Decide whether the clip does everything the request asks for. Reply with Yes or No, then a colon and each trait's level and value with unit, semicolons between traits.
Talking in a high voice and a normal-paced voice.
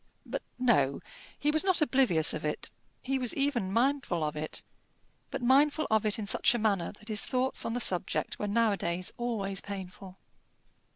Yes: high, 220 Hz; average, 175 wpm